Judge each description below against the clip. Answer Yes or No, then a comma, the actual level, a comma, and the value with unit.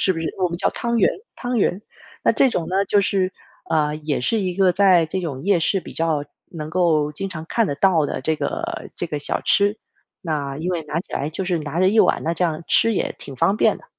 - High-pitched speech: No, medium, 175 Hz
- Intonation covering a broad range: No, average, 3.9 semitones